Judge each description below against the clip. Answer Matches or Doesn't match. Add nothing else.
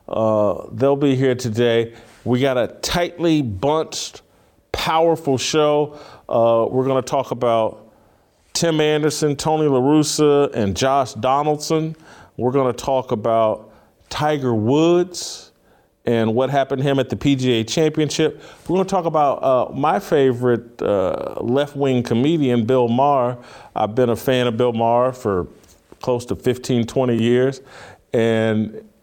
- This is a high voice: Doesn't match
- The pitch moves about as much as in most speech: Matches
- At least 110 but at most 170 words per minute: Matches